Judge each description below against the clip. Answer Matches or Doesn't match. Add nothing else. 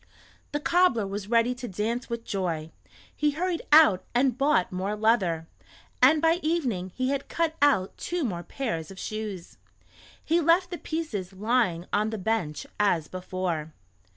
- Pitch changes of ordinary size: Doesn't match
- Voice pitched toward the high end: Matches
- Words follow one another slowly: Doesn't match